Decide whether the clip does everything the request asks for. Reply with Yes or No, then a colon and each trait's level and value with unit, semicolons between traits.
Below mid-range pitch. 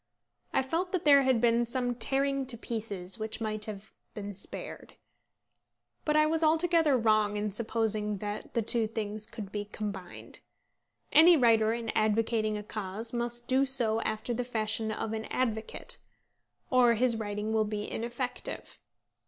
No: high, 225 Hz